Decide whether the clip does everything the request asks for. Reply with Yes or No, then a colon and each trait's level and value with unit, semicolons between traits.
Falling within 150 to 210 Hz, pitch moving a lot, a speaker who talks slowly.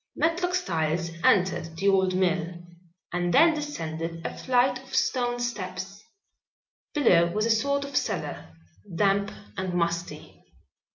Yes: high, 190 Hz; wide, 6.3 semitones; slow, 125 wpm